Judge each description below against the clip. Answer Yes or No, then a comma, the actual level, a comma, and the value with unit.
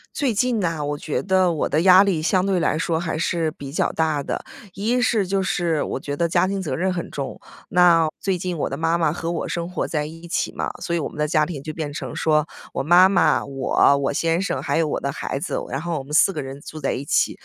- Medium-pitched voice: Yes, medium, 165 Hz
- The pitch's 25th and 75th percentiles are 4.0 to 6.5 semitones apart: No, average, 3.3 semitones